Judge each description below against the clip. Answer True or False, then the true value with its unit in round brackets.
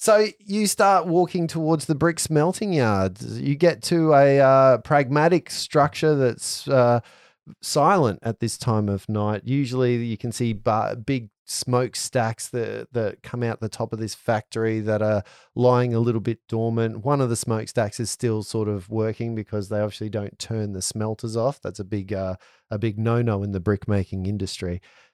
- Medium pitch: False (115 Hz)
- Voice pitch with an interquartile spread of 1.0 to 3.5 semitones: False (4.3 semitones)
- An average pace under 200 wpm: True (185 wpm)